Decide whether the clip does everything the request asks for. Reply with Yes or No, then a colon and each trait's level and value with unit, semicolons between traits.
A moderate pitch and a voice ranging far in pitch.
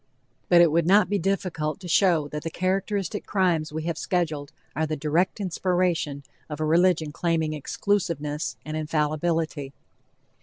No: medium, 165 Hz; average, 3.1 semitones